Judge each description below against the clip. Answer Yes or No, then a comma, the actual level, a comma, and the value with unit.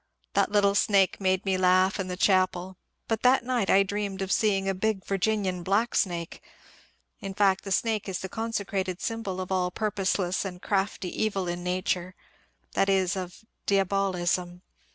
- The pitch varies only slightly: Yes, narrow, 1.7 semitones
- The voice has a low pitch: No, high, 190 Hz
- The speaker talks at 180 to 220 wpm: No, average, 170 wpm